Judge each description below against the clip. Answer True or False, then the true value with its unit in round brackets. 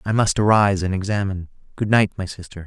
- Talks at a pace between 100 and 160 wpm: False (205 wpm)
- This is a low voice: True (100 Hz)